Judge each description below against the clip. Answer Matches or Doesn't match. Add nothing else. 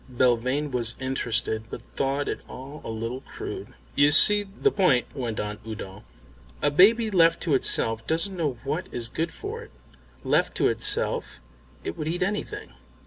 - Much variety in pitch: Matches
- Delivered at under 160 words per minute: Doesn't match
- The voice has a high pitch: Doesn't match